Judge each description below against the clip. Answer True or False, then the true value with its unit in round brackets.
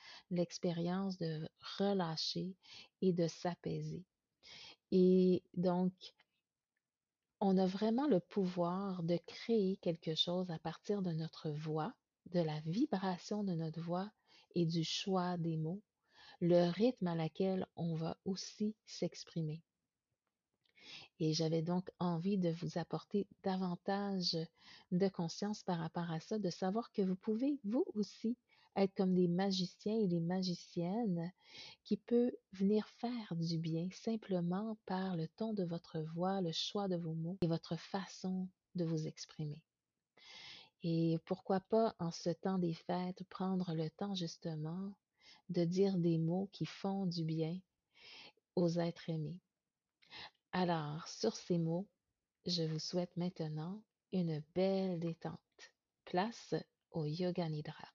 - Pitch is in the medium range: True (180 Hz)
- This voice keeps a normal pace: False (135 wpm)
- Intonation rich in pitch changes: False (2.8 semitones)